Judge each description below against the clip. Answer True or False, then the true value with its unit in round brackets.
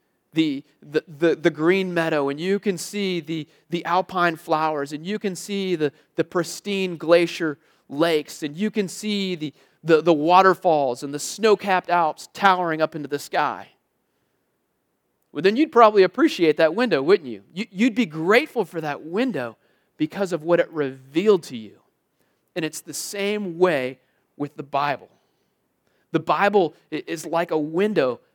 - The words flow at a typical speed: True (165 wpm)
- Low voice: False (170 Hz)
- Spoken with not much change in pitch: False (4.3 semitones)